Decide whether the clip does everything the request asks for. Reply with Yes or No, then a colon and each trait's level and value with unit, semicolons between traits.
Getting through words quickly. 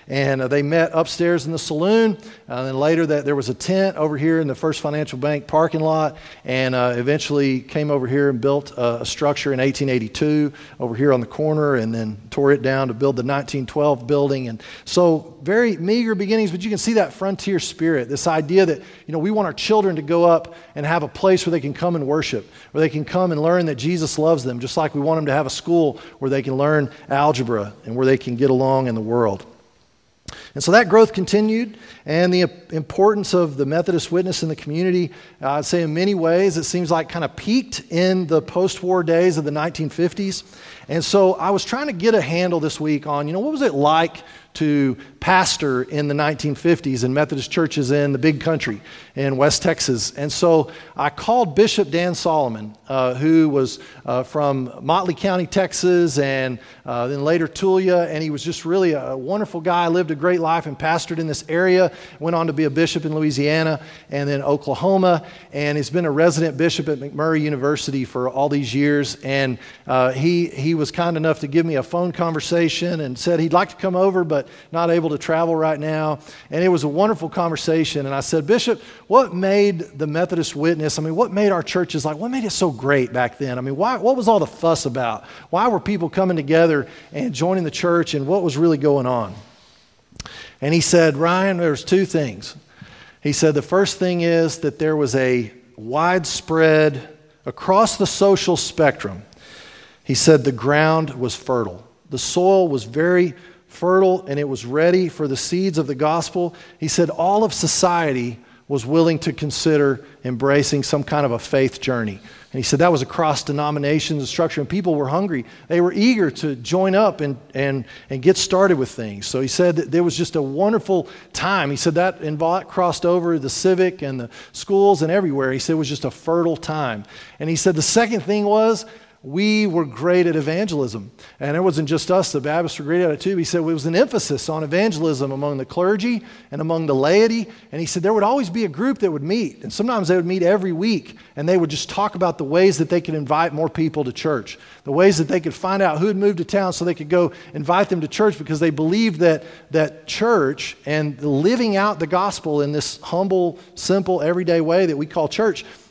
Yes: fast, 215 wpm